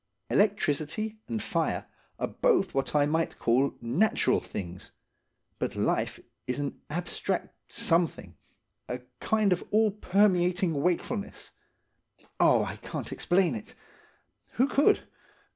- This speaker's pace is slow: Yes, slow, 110 wpm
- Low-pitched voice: No, medium, 180 Hz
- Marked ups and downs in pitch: Yes, wide, 6.6 semitones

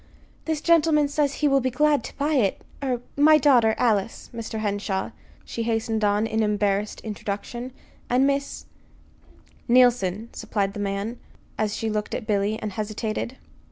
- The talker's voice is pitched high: Yes, high, 225 Hz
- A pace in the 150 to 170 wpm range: Yes, average, 155 wpm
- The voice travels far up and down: No, average, 4.4 semitones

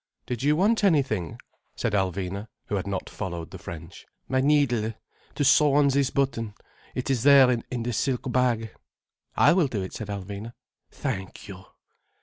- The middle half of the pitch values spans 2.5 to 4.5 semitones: No, wide, 5.6 semitones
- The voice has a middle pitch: No, low, 120 Hz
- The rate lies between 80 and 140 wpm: No, average, 165 wpm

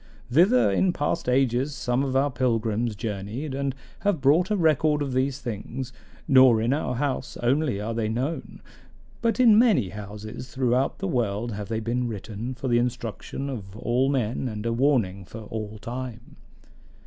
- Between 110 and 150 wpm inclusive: No, average, 170 wpm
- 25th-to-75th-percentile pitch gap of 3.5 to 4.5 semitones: Yes, average, 3.9 semitones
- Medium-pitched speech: No, low, 125 Hz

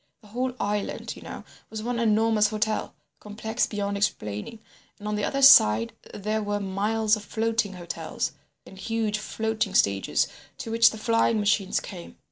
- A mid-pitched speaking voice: No, high, 215 Hz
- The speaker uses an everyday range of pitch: No, narrow, 1.7 semitones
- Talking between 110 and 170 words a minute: Yes, average, 160 wpm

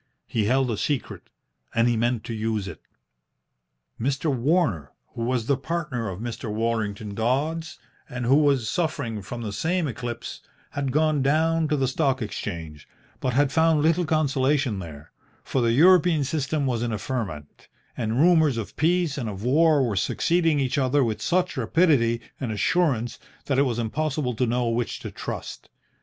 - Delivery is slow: No, average, 170 wpm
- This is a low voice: Yes, low, 130 Hz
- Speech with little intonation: No, average, 5.1 semitones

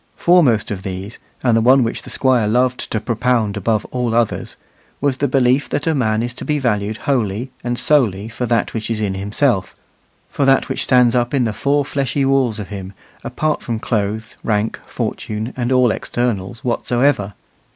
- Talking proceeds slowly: No, average, 190 wpm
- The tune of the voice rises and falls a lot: No, average, 3.4 semitones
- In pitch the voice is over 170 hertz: No, low, 120 Hz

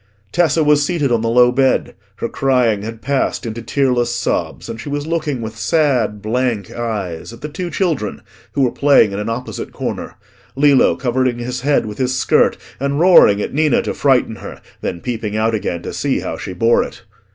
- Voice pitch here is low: Yes, low, 125 Hz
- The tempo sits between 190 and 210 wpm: Yes, average, 195 wpm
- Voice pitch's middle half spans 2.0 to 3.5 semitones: No, average, 4.2 semitones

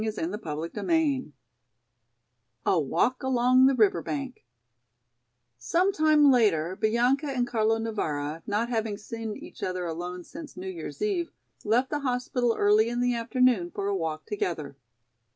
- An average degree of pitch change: No, wide, 5.8 semitones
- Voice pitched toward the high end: Yes, high, 225 Hz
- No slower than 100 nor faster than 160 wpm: Yes, average, 140 wpm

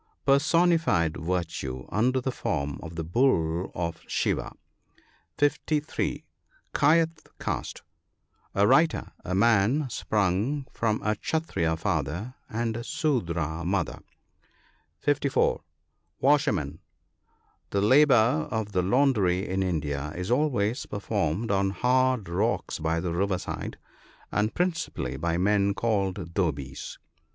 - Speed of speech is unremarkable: No, slow, 125 wpm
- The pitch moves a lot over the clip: Yes, wide, 7.5 semitones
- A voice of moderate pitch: No, low, 100 Hz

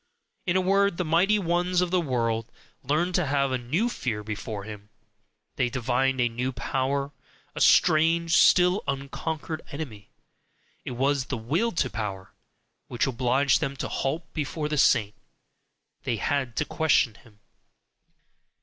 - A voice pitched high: No, medium, 140 Hz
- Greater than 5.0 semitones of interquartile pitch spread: Yes, wide, 5.4 semitones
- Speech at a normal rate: Yes, average, 150 wpm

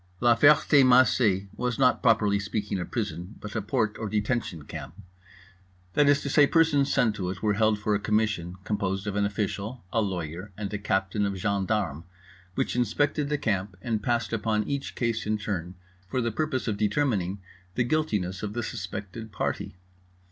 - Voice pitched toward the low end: Yes, low, 105 Hz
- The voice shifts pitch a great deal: No, average, 3.5 semitones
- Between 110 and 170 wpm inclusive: No, average, 180 wpm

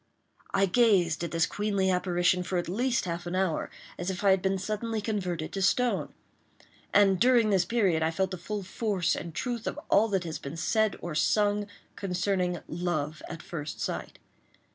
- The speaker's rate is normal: Yes, average, 185 wpm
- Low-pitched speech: No, high, 190 Hz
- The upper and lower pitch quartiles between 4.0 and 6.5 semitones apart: No, average, 3.0 semitones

